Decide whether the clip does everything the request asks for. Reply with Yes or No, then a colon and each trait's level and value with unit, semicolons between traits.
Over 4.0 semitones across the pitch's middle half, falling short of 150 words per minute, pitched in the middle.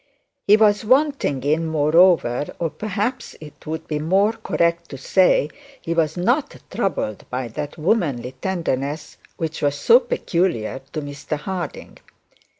Yes: wide, 5.4 semitones; average, 140 wpm; medium, 165 Hz